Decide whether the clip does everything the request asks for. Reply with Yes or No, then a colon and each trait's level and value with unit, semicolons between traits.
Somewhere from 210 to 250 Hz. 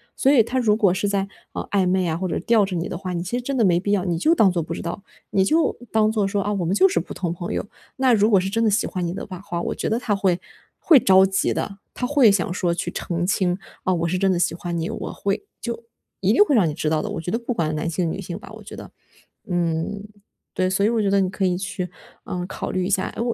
No: high, 190 Hz